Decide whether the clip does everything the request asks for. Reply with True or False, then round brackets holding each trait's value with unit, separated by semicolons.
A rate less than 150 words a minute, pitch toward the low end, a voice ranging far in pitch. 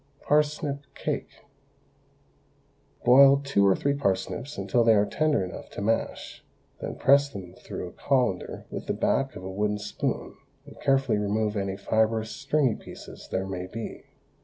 False (155 wpm; 110 Hz; 5.9 semitones)